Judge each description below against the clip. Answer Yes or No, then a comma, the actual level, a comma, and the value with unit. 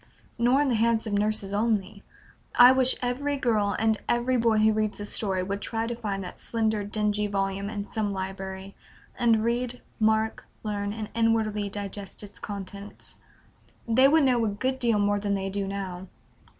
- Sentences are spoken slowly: No, average, 175 wpm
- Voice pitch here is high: Yes, high, 215 Hz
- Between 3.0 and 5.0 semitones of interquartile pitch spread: No, narrow, 2.5 semitones